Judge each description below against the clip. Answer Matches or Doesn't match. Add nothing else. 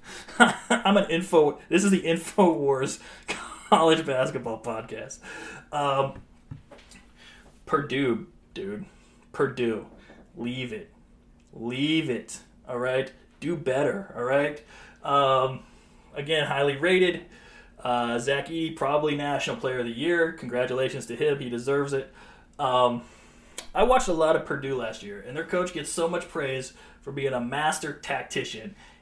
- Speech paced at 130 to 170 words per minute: Matches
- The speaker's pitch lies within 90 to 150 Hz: Matches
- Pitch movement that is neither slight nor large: Matches